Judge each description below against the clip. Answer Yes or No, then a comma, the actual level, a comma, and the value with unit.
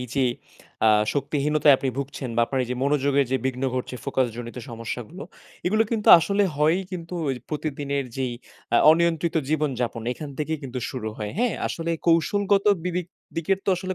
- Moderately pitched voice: Yes, medium, 145 Hz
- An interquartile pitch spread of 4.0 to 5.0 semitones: Yes, average, 4.5 semitones